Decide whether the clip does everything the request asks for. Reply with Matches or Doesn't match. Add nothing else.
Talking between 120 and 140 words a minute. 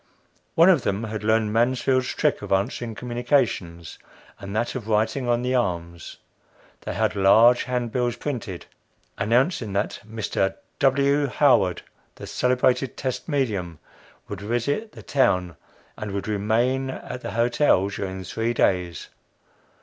Matches